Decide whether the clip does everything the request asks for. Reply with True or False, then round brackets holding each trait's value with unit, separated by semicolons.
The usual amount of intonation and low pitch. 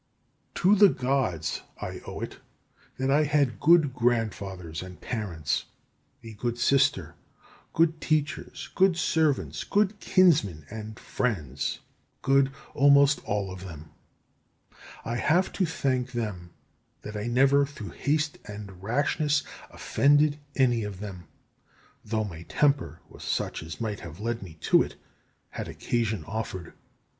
False (6.5 semitones; 120 Hz)